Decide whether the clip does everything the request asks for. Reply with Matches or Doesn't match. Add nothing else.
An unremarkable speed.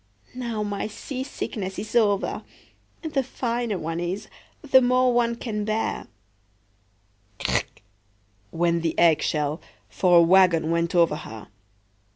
Doesn't match